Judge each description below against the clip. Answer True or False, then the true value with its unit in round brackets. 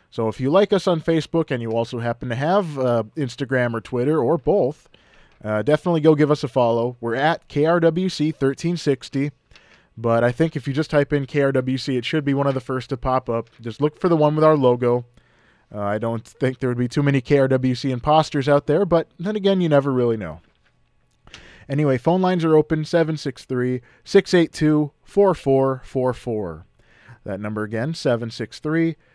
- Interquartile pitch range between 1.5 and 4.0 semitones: False (4.6 semitones)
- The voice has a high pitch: False (135 Hz)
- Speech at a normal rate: True (180 wpm)